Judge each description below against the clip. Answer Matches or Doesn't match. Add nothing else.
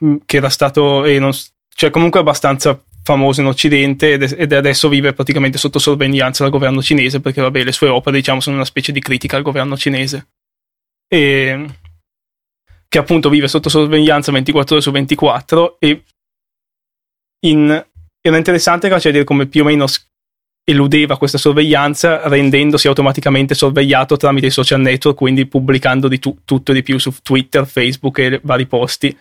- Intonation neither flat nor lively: Doesn't match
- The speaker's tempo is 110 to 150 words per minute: Doesn't match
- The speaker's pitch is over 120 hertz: Matches